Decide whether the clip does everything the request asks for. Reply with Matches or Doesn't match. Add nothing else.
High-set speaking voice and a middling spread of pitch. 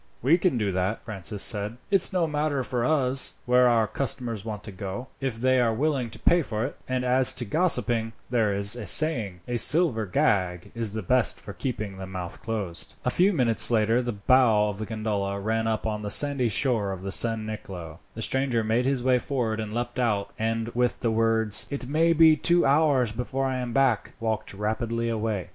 Doesn't match